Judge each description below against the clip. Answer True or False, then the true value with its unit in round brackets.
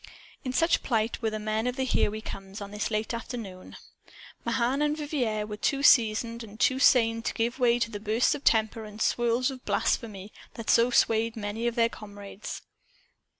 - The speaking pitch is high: True (230 Hz)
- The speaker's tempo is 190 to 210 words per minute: True (195 wpm)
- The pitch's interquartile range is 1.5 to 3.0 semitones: True (2.4 semitones)